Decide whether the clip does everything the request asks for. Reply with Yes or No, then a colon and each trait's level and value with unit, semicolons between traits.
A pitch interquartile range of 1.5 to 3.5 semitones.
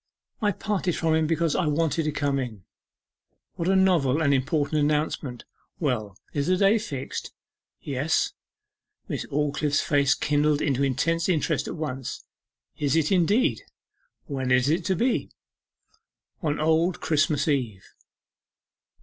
Yes: average, 3.1 semitones